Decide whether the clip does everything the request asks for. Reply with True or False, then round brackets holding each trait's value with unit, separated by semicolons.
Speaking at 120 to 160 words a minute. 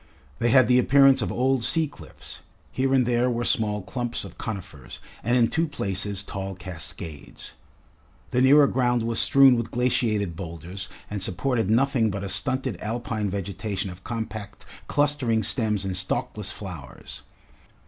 True (150 wpm)